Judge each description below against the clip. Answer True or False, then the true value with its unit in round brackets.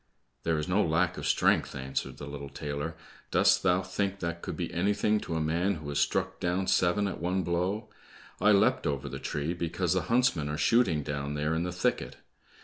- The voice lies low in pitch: True (85 Hz)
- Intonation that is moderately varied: True (4.2 semitones)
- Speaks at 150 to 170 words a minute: False (205 wpm)